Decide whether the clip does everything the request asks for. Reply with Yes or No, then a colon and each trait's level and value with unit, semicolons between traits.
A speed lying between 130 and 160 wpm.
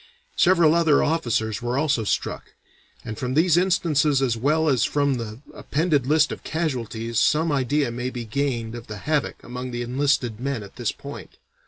No: average, 175 wpm